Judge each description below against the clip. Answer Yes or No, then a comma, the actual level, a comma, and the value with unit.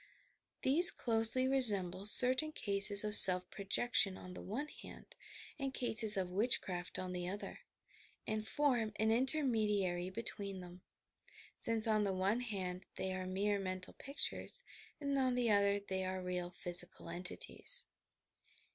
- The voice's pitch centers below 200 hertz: No, high, 205 Hz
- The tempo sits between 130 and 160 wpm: Yes, average, 145 wpm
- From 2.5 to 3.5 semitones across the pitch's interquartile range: No, average, 4.4 semitones